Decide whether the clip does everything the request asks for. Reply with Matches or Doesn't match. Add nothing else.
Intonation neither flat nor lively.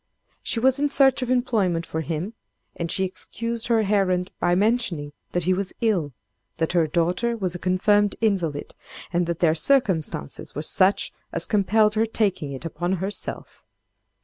Matches